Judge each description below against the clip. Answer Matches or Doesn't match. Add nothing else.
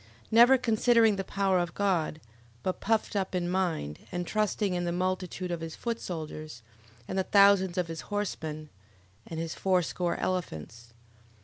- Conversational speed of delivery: Matches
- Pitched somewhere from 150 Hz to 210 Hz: Matches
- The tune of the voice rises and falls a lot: Doesn't match